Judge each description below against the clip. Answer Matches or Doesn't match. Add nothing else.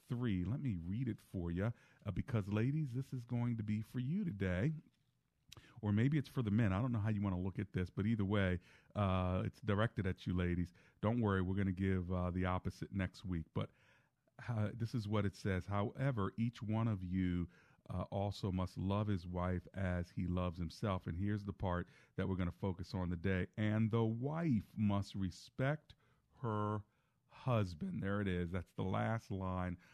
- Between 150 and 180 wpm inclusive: Doesn't match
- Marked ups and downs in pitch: Doesn't match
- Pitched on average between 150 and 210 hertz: Doesn't match